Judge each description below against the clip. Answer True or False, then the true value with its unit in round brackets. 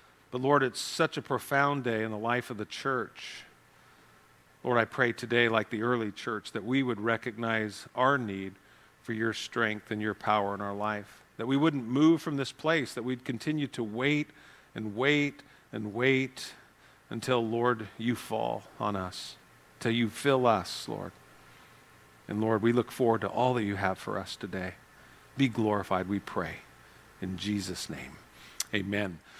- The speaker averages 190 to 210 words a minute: False (170 wpm)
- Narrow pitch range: False (3.5 semitones)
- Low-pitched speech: True (115 Hz)